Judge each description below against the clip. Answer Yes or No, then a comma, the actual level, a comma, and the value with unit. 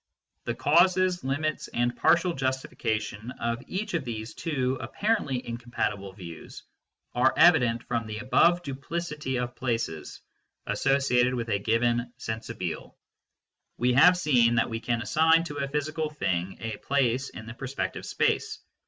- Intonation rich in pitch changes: No, average, 4.6 semitones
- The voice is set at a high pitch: No, low, 125 Hz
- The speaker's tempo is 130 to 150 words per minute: Yes, average, 145 wpm